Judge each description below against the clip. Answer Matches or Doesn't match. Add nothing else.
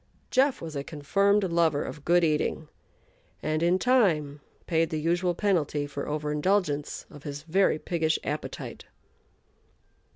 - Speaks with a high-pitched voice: Doesn't match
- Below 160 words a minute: Matches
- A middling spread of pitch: Matches